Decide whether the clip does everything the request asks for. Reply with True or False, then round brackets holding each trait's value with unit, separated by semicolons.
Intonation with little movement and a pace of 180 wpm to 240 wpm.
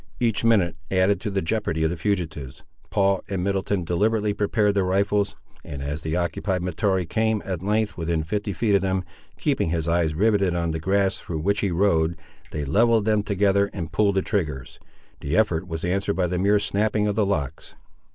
False (3.4 semitones; 195 wpm)